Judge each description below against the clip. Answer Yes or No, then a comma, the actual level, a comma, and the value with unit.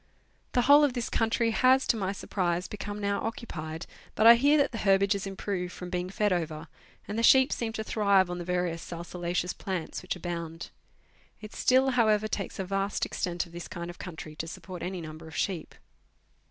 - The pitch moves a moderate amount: Yes, average, 4.2 semitones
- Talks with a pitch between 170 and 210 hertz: Yes, high, 190 Hz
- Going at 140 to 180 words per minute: No, average, 200 wpm